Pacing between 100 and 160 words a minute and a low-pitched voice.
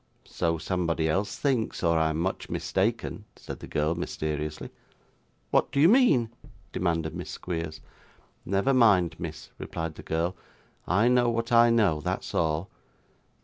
Yes: average, 145 wpm; very low, 90 Hz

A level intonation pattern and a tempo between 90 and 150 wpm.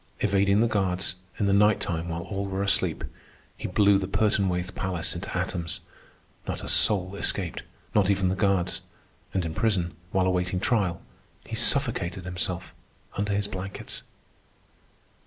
Yes: narrow, 2.0 semitones; average, 145 wpm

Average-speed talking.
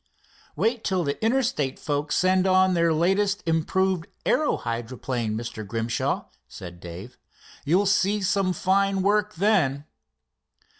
No: slow, 120 wpm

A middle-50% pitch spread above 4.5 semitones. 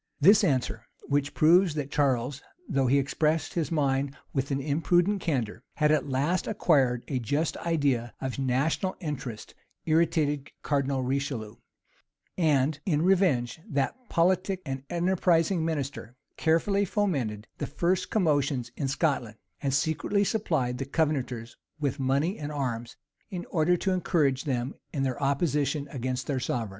No: average, 4.0 semitones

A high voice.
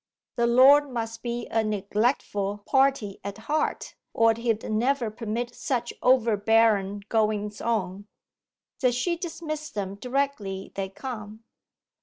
Yes: high, 225 Hz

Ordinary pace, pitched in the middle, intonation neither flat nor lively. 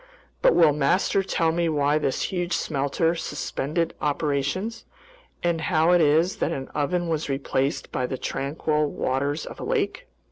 Yes: average, 155 wpm; medium, 155 Hz; average, 3.2 semitones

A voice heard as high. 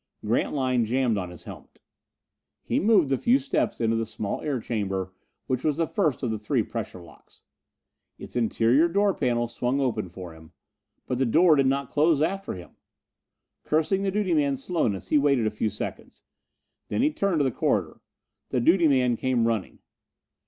No: low, 130 Hz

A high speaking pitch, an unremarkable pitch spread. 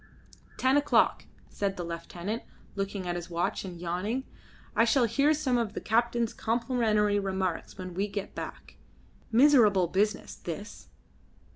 Yes: high, 205 Hz; average, 4.3 semitones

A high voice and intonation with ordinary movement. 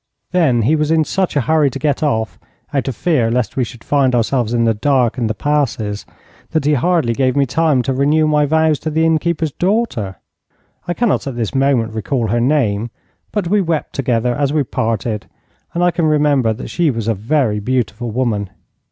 No: low, 135 Hz; average, 5.0 semitones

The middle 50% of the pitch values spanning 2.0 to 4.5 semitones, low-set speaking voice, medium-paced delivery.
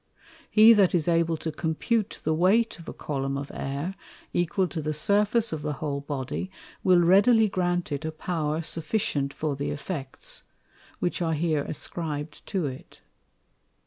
No: average, 3.9 semitones; medium, 160 Hz; average, 160 wpm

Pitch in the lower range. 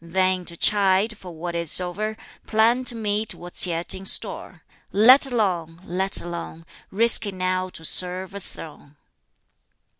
No: medium, 185 Hz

